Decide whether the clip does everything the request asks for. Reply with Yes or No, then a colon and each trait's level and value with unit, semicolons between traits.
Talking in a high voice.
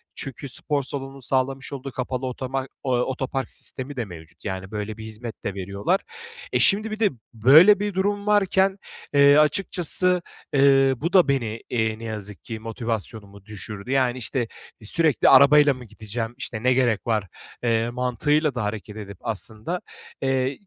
No: low, 130 Hz